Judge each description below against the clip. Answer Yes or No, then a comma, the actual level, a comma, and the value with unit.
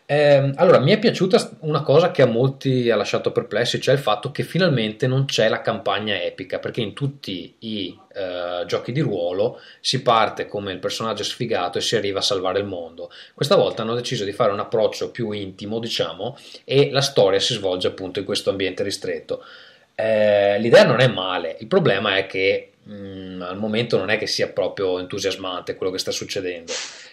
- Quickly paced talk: Yes, fast, 190 wpm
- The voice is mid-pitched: Yes, medium, 145 Hz